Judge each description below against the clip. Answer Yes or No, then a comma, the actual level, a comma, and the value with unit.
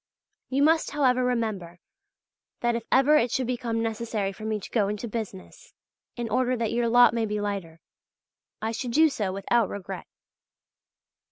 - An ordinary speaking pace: Yes, average, 165 wpm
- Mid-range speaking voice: No, high, 230 Hz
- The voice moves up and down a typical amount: Yes, average, 3.2 semitones